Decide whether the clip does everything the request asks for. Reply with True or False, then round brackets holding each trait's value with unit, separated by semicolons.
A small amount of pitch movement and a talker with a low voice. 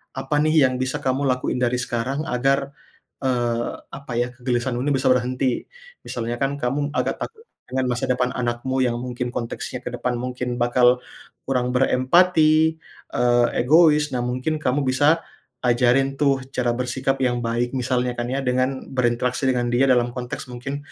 True (1.9 semitones; 125 Hz)